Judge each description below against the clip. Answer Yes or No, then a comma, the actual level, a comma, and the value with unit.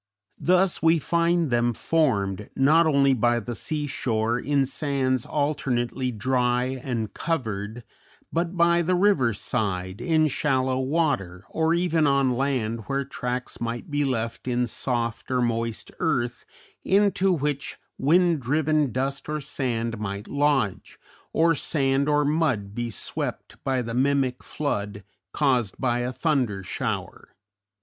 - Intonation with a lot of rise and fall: No, average, 4.3 semitones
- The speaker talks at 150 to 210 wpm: No, slow, 135 wpm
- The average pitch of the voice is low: Yes, low, 130 Hz